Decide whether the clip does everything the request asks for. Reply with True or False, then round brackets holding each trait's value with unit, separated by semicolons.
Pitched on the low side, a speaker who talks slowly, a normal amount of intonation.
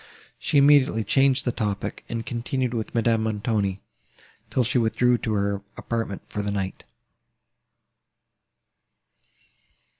True (115 Hz; 115 wpm; 3.2 semitones)